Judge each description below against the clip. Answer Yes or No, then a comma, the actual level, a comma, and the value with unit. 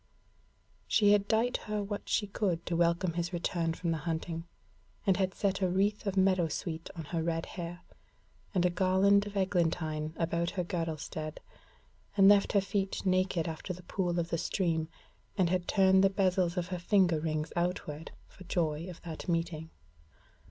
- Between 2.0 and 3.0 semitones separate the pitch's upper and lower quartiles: Yes, narrow, 2.6 semitones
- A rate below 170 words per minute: No, average, 175 wpm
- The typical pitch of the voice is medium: Yes, medium, 175 Hz